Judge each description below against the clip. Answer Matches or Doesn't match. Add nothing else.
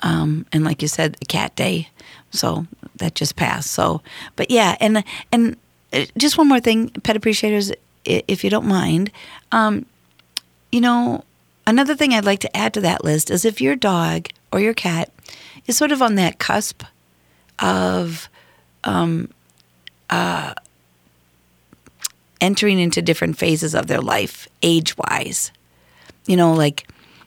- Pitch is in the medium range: Matches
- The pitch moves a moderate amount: Doesn't match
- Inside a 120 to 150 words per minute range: Matches